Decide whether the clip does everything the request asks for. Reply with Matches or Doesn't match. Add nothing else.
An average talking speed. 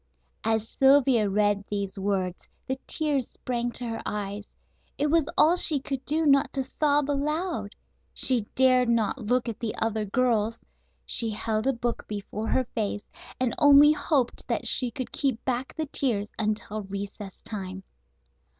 Matches